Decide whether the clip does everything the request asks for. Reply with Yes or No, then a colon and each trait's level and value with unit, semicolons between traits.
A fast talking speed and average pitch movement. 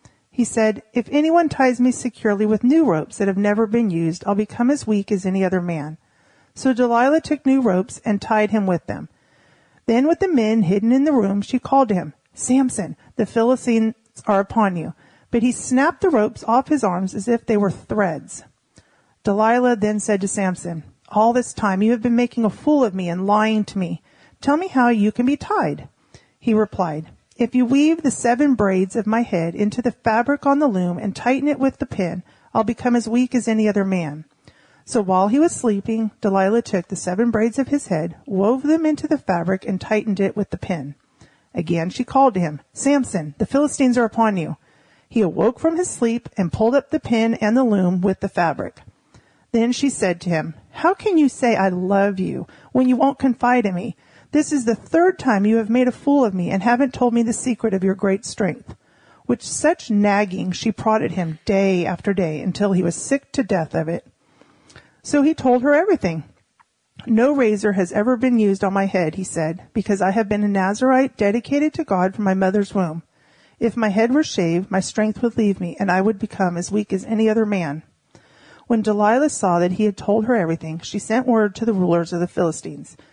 Yes: fast, 215 wpm; average, 4.6 semitones